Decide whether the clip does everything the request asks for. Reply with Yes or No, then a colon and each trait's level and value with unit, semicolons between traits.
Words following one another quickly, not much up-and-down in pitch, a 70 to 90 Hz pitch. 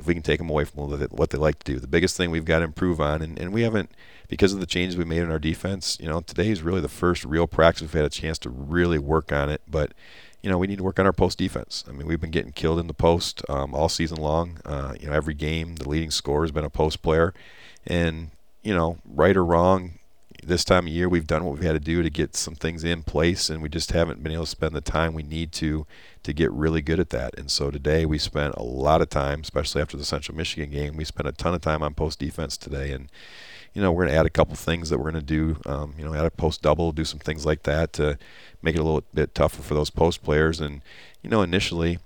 Yes: fast, 280 wpm; narrow, 2.1 semitones; very low, 80 Hz